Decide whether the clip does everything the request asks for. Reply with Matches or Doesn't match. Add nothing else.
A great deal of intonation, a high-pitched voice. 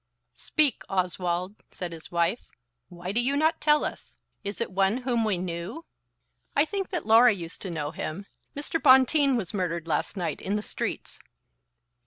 Matches